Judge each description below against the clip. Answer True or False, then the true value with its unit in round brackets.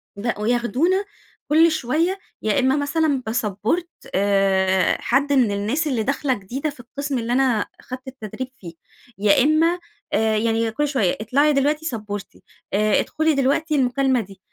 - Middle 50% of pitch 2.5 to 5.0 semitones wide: False (5.4 semitones)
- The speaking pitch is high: True (255 Hz)